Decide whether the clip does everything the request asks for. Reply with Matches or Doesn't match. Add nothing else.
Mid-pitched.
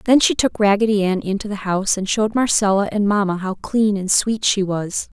Doesn't match